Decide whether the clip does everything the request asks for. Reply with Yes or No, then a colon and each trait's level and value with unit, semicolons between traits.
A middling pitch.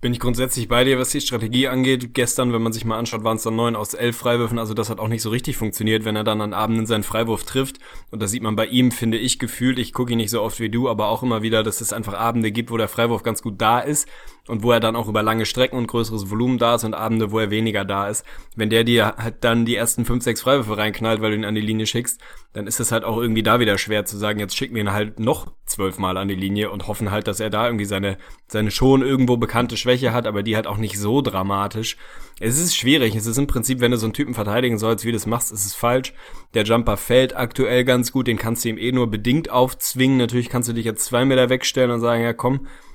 No: low, 115 Hz